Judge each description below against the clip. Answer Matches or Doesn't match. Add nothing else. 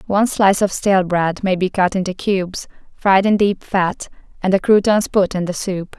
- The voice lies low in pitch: Doesn't match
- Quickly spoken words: Matches